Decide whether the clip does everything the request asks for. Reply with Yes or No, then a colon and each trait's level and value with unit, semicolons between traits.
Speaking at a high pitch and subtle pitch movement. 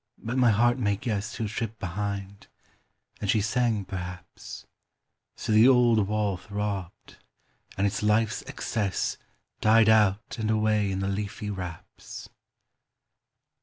No: low, 105 Hz; narrow, 2.1 semitones